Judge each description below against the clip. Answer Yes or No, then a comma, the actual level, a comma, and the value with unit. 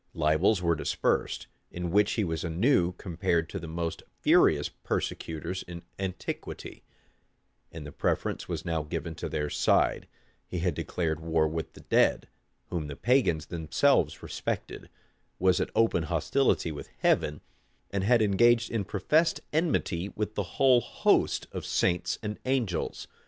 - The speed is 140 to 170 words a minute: Yes, average, 145 wpm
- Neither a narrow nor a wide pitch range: Yes, average, 4.5 semitones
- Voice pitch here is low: Yes, very low, 90 Hz